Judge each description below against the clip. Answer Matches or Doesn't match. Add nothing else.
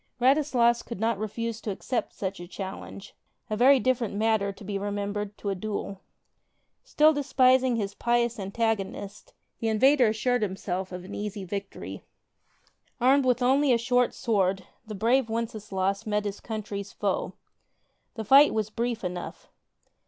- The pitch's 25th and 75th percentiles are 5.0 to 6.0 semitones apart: Doesn't match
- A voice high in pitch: Matches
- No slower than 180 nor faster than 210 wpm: Doesn't match